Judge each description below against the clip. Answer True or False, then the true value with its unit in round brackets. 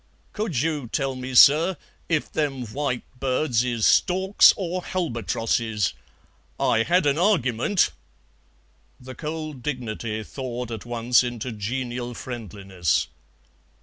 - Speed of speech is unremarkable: False (115 wpm)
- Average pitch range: True (4.7 semitones)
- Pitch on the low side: True (125 Hz)